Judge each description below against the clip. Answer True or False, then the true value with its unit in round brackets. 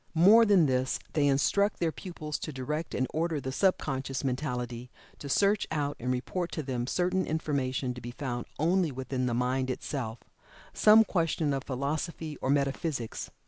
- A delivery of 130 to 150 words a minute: False (170 wpm)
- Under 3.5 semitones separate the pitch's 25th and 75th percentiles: False (4.3 semitones)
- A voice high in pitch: False (140 Hz)